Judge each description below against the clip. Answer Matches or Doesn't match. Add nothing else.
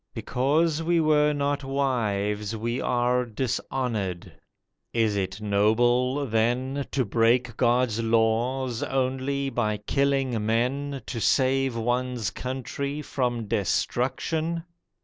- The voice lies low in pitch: Matches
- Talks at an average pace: Doesn't match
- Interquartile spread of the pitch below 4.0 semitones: Matches